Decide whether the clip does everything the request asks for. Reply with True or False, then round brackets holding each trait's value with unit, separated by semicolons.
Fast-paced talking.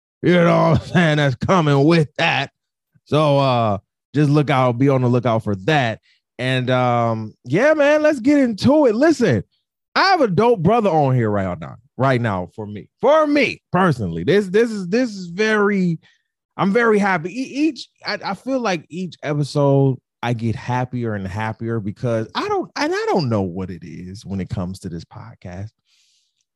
False (185 wpm)